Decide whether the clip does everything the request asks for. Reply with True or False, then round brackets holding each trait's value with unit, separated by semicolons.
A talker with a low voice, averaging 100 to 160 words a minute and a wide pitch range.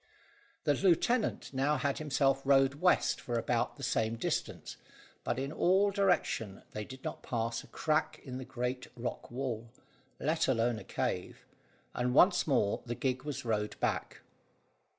False (130 Hz; 155 wpm; 4.0 semitones)